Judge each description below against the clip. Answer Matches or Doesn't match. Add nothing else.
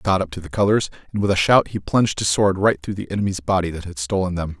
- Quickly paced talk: Matches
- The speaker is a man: Matches